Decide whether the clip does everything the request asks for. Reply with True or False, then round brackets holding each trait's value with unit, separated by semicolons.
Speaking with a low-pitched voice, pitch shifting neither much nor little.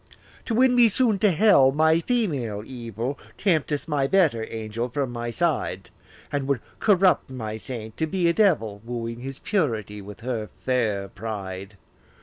False (130 Hz; 7.2 semitones)